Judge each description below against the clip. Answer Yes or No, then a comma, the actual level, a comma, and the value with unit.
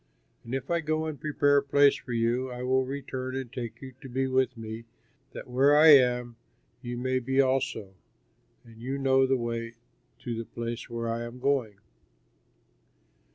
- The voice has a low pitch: Yes, low, 130 Hz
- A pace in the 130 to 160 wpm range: No, average, 180 wpm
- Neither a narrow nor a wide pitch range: No, narrow, 2.3 semitones